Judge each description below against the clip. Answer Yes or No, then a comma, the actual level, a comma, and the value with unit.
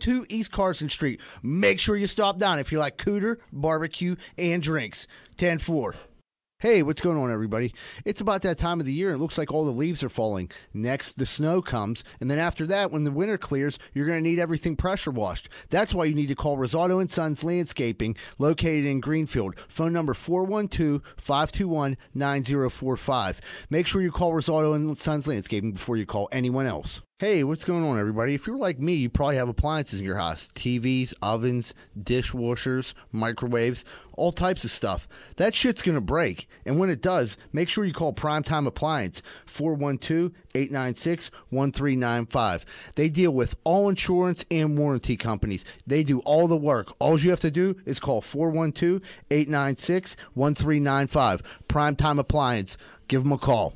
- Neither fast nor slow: Yes, average, 175 wpm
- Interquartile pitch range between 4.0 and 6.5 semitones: Yes, average, 4.9 semitones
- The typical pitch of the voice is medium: Yes, medium, 150 Hz